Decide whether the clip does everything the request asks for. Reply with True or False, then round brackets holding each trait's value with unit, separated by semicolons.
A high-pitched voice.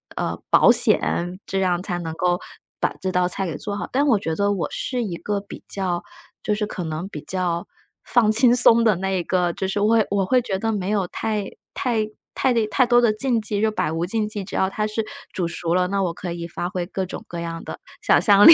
True (195 Hz)